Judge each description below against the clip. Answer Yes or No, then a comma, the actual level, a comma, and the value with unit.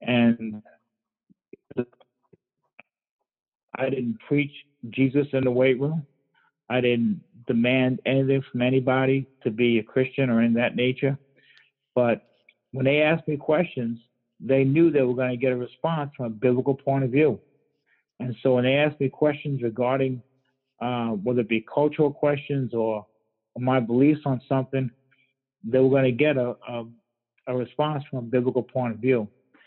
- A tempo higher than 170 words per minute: No, average, 160 wpm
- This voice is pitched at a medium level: No, low, 130 Hz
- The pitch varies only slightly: Yes, narrow, 2.0 semitones